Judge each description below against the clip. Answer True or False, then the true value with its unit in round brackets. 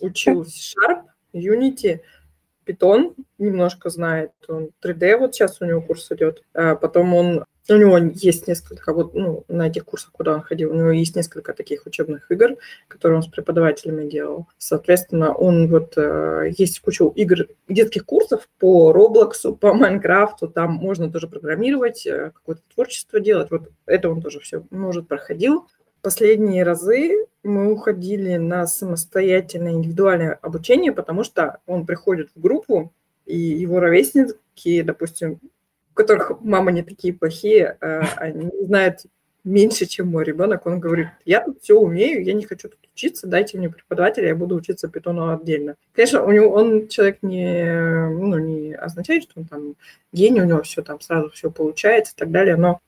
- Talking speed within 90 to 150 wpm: False (160 wpm)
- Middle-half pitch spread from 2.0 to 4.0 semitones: False (4.4 semitones)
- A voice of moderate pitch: True (180 Hz)